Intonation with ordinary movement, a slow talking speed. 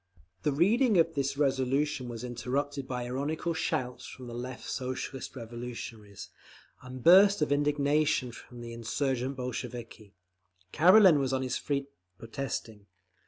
Yes: average, 3.1 semitones; slow, 130 wpm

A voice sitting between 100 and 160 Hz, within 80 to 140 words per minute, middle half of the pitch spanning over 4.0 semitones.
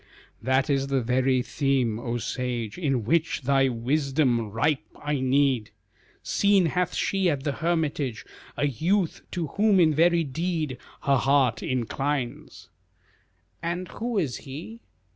Yes: medium, 140 Hz; slow, 135 wpm; average, 4.5 semitones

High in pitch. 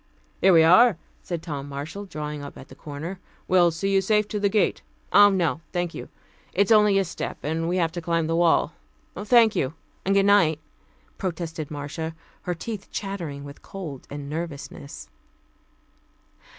No: medium, 170 Hz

